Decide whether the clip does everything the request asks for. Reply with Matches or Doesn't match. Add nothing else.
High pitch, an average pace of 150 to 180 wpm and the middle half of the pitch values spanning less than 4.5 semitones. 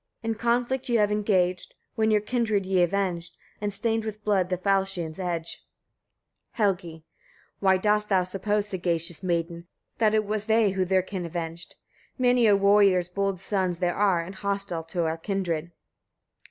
Matches